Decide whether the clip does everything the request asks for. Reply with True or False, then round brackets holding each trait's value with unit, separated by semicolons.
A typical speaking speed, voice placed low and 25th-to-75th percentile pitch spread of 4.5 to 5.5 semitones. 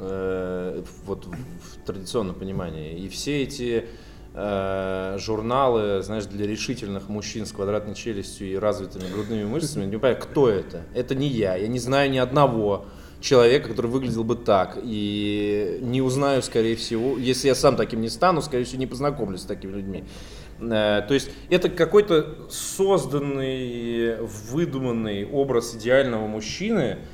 True (145 wpm; 115 Hz; 4.9 semitones)